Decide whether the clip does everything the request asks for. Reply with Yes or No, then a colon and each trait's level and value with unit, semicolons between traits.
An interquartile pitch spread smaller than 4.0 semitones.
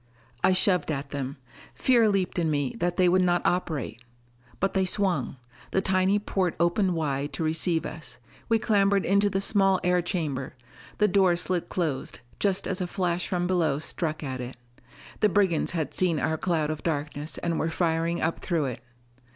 Yes: average, 3.3 semitones